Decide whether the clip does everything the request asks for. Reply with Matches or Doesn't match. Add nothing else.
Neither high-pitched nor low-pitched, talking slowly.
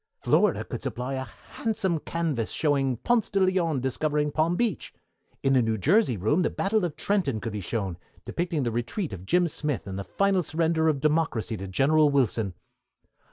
Doesn't match